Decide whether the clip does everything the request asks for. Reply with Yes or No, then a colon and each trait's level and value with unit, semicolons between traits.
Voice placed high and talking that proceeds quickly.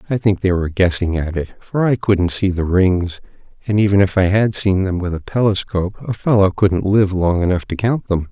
No: very low, 95 Hz; fast, 230 wpm